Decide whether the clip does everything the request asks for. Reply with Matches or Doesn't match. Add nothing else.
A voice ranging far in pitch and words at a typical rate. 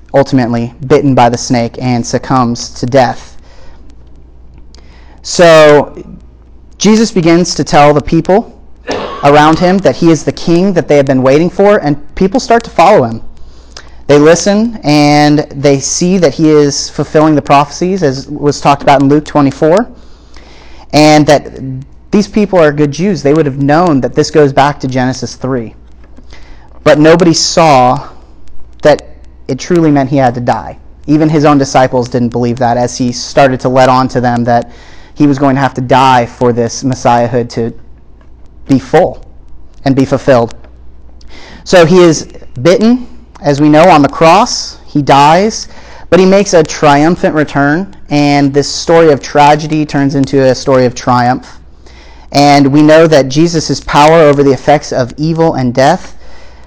Doesn't match